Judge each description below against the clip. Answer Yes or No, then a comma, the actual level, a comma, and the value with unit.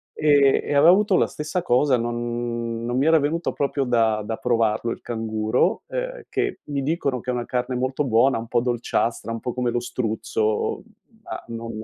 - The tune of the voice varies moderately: Yes, average, 3.6 semitones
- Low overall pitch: Yes, low, 125 Hz